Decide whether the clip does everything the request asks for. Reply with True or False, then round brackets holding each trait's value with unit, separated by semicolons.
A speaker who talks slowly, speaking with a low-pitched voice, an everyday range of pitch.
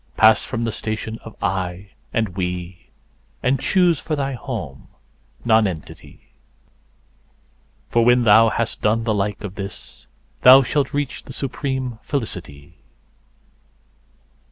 True (115 wpm; 110 Hz; 4.8 semitones)